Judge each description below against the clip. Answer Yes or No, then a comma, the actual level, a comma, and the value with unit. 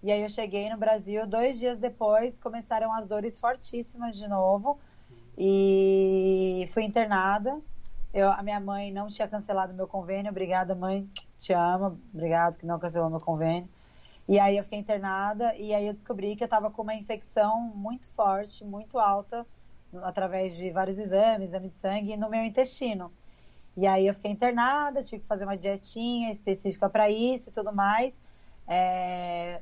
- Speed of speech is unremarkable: Yes, average, 170 wpm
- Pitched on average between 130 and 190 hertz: No, high, 205 Hz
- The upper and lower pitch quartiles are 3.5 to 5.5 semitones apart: No, average, 2.8 semitones